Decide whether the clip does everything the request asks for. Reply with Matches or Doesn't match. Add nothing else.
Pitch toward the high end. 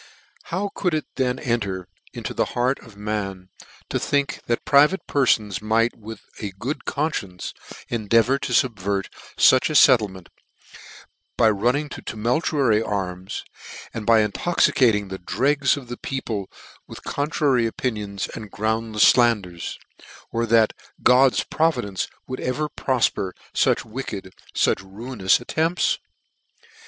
Doesn't match